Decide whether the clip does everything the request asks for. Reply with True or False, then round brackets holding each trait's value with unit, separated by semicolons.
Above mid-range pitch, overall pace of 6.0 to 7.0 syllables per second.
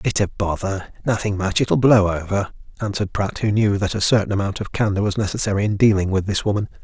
False (100 Hz; 6.1 syllables/s)